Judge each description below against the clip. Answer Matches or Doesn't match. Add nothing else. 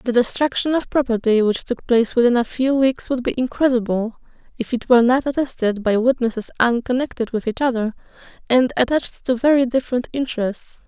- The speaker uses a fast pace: Doesn't match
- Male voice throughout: Doesn't match